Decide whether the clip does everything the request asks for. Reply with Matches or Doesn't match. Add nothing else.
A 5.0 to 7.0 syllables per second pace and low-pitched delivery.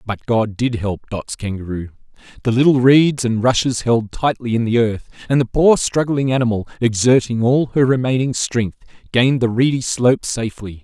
Matches